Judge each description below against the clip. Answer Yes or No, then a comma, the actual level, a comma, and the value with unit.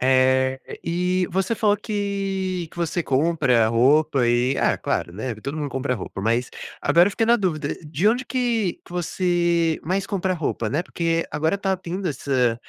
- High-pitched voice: No, medium, 165 Hz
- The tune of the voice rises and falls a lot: Yes, wide, 6.2 semitones